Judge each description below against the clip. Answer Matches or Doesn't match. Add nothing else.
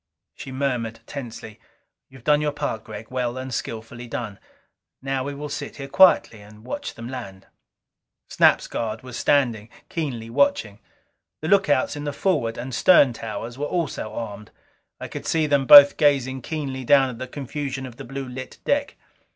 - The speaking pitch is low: Matches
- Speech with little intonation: Doesn't match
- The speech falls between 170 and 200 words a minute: Matches